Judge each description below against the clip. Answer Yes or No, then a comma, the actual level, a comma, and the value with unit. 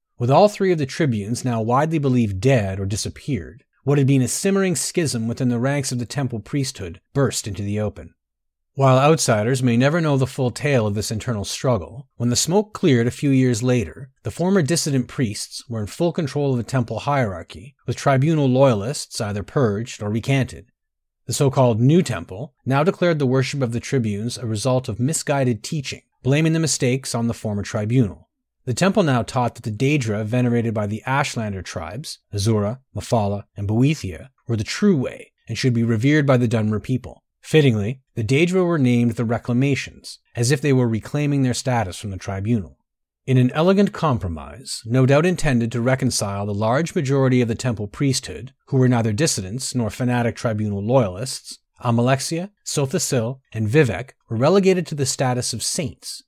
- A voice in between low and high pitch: No, low, 125 Hz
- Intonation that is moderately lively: Yes, average, 3.8 semitones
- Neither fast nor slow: Yes, average, 185 wpm